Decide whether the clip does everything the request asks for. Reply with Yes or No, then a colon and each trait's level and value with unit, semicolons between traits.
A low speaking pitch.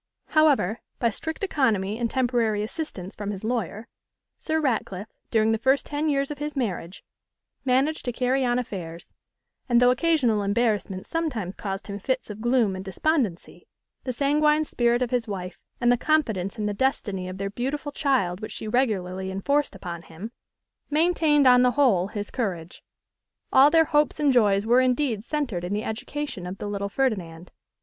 No: high, 235 Hz